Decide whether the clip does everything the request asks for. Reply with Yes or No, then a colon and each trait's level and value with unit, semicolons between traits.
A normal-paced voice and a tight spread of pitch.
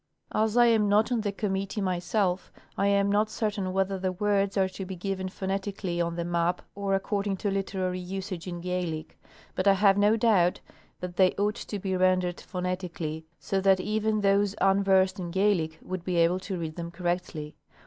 Yes: average, 190 wpm; narrow, 1.9 semitones